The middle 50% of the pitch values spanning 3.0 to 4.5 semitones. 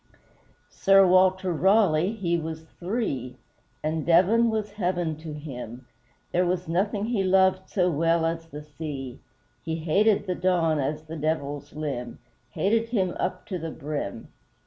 Yes: average, 3.6 semitones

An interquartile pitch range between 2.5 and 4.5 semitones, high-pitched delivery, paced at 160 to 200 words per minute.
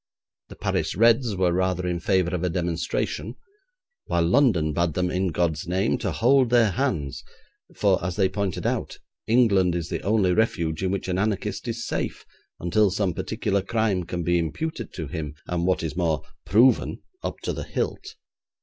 No: average, 4.0 semitones; very low, 95 Hz; average, 175 wpm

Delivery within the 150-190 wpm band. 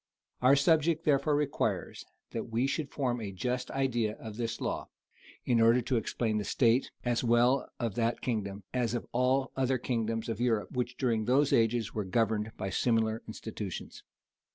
Yes: average, 170 wpm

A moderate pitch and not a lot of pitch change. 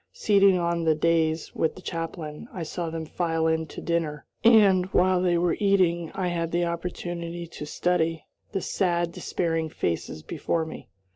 Yes: medium, 170 Hz; narrow, 1.7 semitones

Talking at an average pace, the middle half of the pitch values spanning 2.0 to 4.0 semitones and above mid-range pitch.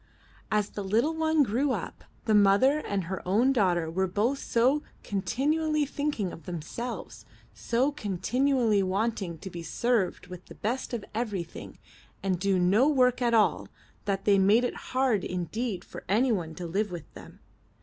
No: average, 170 wpm; average, 5.2 semitones; high, 215 Hz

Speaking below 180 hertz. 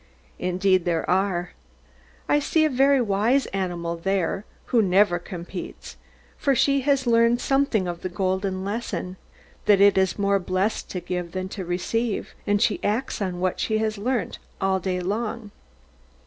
No: high, 195 Hz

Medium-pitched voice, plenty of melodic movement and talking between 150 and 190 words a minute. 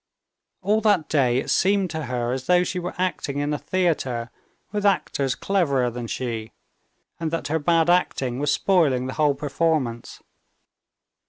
Yes: medium, 150 Hz; wide, 5.8 semitones; average, 160 wpm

